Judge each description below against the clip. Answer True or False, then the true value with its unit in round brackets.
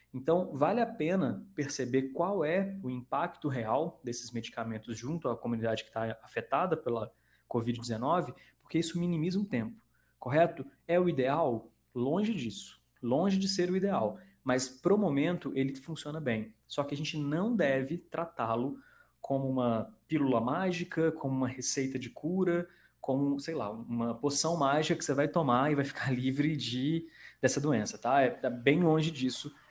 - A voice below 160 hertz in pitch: True (140 Hz)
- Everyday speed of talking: True (165 wpm)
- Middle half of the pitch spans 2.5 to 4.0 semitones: False (4.8 semitones)